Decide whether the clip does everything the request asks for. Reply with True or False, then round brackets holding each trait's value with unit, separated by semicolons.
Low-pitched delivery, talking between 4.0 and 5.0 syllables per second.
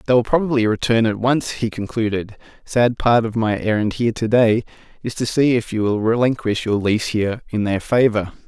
False (115 Hz; 5.5 syllables/s)